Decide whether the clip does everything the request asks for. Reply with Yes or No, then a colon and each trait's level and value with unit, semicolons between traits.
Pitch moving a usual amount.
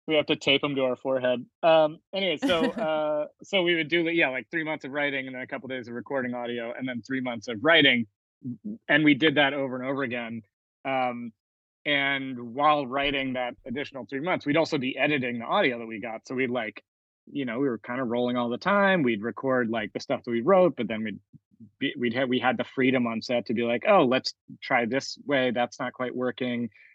Yes: average, 3.5 semitones